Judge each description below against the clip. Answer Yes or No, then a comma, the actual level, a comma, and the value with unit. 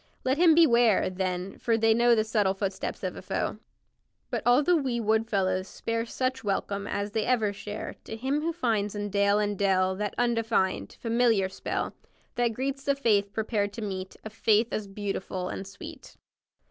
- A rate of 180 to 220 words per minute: Yes, average, 185 wpm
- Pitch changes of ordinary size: Yes, average, 3.2 semitones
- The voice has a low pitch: No, high, 215 Hz